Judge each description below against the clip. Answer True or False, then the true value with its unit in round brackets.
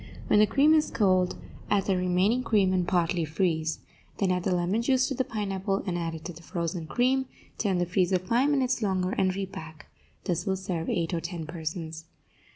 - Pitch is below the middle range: False (185 Hz)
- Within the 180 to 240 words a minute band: True (200 wpm)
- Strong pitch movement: False (3.4 semitones)